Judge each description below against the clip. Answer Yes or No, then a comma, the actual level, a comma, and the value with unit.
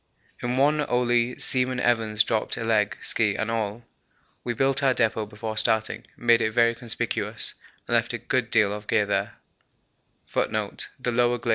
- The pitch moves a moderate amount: No, narrow, 1.9 semitones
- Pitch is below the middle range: Yes, low, 115 Hz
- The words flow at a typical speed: Yes, average, 150 wpm